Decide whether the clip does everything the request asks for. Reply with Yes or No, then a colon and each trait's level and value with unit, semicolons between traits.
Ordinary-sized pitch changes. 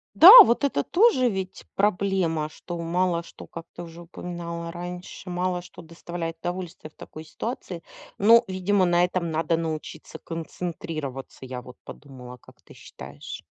No: narrow, 2.3 semitones